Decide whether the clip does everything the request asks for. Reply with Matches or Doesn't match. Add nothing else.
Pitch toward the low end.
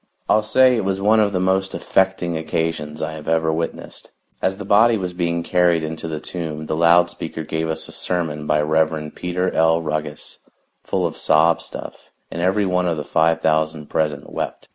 Matches